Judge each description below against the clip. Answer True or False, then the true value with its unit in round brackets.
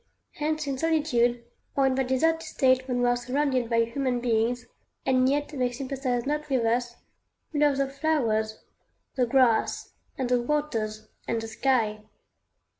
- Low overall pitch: False (255 Hz)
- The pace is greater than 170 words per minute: False (160 wpm)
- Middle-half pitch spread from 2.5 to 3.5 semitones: True (2.9 semitones)